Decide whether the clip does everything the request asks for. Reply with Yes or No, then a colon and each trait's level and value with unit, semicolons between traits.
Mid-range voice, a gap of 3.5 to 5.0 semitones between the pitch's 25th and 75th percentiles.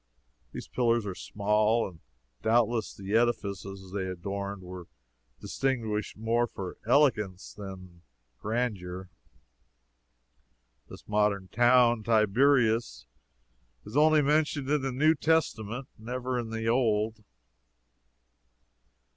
No: low, 110 Hz; average, 3.9 semitones